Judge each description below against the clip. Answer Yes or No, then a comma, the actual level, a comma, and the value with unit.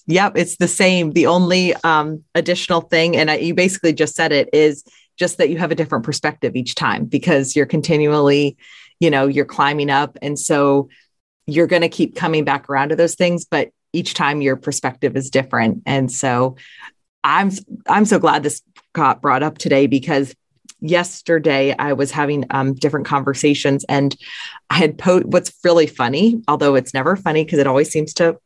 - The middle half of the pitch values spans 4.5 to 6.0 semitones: No, average, 3.4 semitones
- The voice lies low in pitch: No, medium, 155 Hz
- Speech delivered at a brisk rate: No, average, 185 wpm